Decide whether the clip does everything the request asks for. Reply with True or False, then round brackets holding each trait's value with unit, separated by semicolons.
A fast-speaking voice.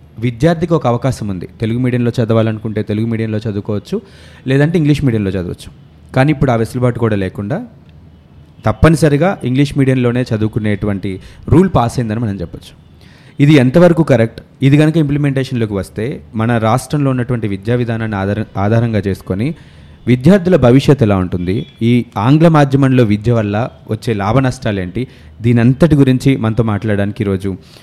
True (135 wpm)